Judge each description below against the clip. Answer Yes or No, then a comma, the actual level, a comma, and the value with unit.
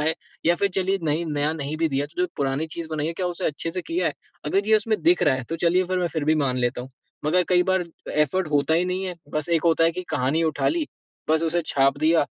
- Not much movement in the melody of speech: No, average, 3.3 semitones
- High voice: No, medium, 165 Hz